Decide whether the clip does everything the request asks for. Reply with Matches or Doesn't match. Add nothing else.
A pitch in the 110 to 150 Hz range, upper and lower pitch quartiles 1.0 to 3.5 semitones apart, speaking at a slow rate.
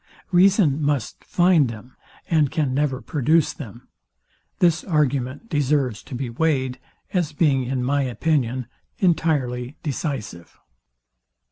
Doesn't match